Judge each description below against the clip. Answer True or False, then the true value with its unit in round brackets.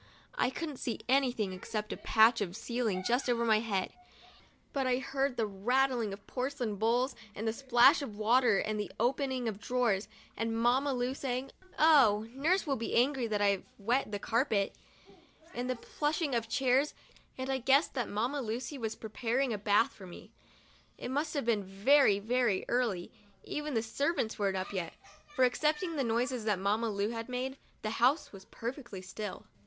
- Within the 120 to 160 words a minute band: False (185 wpm)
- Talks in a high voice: True (240 Hz)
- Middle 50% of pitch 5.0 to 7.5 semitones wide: False (3.9 semitones)